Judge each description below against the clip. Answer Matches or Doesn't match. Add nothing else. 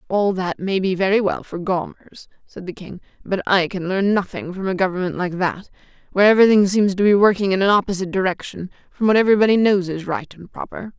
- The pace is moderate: Doesn't match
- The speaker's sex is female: Matches